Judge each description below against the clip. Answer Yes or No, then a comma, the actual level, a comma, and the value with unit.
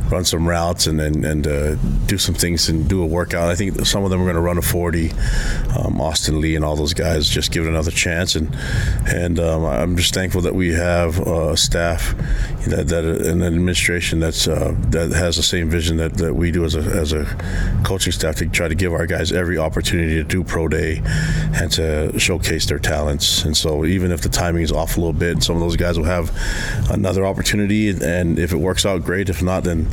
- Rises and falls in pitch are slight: Yes, narrow, 2.3 semitones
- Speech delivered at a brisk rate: Yes, fast, 230 wpm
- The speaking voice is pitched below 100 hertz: Yes, very low, 85 Hz